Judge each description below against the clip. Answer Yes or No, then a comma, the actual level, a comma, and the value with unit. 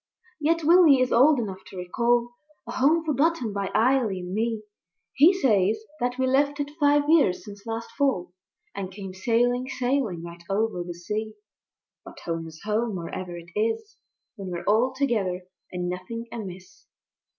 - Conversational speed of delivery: Yes, average, 160 wpm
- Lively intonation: Yes, wide, 6.0 semitones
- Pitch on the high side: Yes, high, 225 Hz